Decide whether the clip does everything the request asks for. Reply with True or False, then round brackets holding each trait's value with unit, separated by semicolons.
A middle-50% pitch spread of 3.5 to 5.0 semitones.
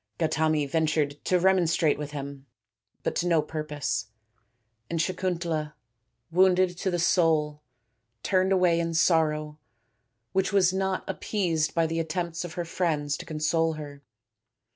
False (2.7 semitones)